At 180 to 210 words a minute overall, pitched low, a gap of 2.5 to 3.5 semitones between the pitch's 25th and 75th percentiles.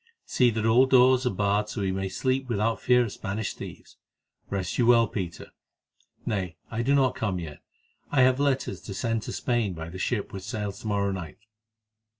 No: average, 200 wpm; low, 110 Hz; average, 4.2 semitones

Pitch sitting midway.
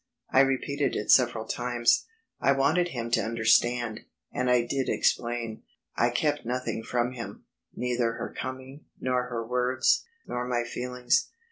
No: low, 125 Hz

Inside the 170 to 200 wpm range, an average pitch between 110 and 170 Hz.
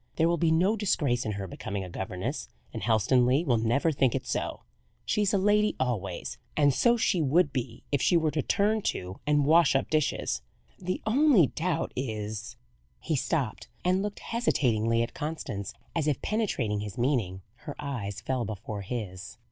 Yes: average, 180 wpm; low, 135 Hz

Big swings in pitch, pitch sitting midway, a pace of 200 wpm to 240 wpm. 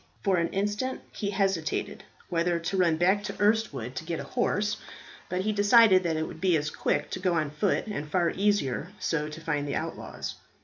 No: average, 4.3 semitones; medium, 180 Hz; fast, 205 wpm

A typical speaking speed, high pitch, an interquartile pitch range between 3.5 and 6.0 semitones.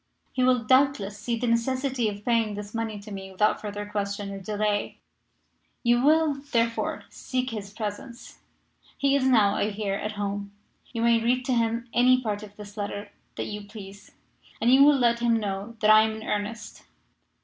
No: average, 185 wpm; high, 220 Hz; average, 2.8 semitones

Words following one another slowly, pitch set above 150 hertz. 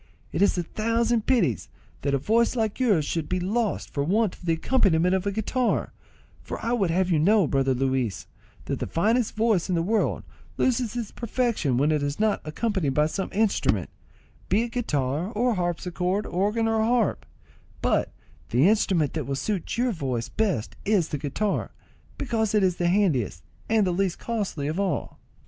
No: average, 185 wpm; high, 190 Hz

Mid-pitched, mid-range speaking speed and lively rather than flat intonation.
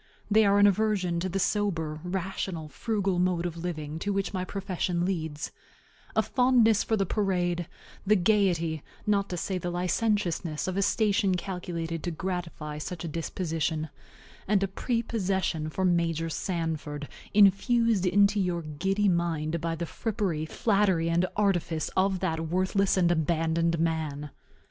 No: medium, 180 Hz; average, 150 wpm; average, 3.3 semitones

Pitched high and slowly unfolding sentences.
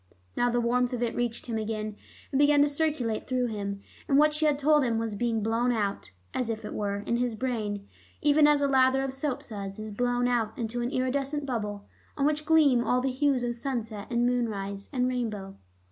No: high, 245 Hz; fast, 205 wpm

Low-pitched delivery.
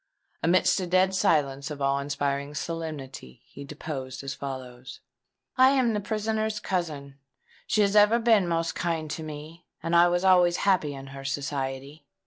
No: medium, 155 Hz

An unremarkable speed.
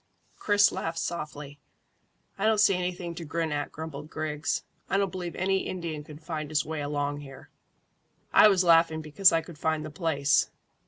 Yes: average, 175 wpm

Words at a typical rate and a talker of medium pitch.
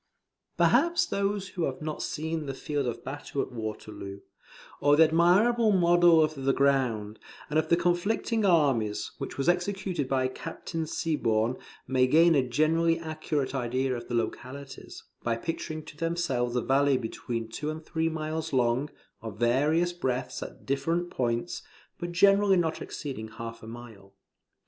Yes: average, 155 wpm; medium, 145 Hz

